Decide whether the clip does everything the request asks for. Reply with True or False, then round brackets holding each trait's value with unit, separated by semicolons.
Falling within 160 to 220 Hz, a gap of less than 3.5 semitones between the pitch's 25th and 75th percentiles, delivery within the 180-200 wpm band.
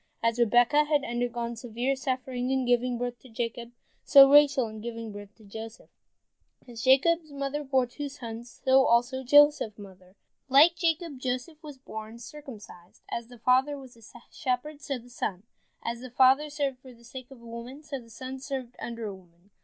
False (250 Hz; 2.9 semitones; 185 wpm)